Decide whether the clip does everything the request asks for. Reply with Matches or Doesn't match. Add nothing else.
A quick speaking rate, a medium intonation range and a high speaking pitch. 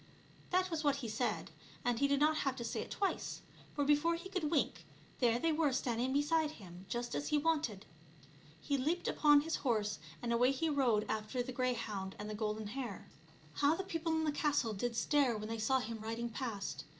Matches